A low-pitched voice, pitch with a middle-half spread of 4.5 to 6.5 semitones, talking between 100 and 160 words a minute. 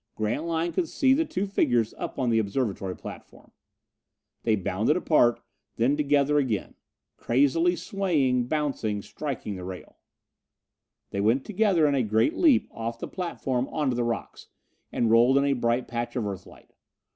Yes: low, 130 Hz; average, 5.2 semitones; average, 155 wpm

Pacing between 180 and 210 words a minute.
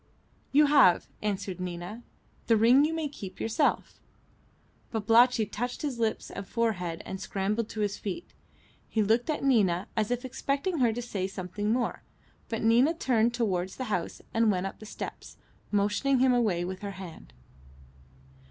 No: average, 160 wpm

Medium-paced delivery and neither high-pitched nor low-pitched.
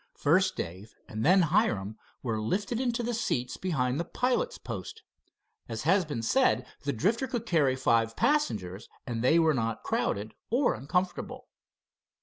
Yes: average, 150 wpm; medium, 155 Hz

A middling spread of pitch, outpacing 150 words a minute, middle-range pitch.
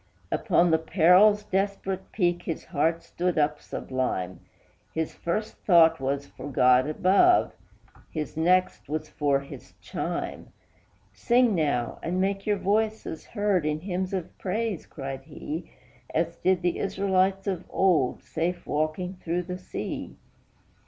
No: average, 3.9 semitones; slow, 135 wpm; medium, 175 Hz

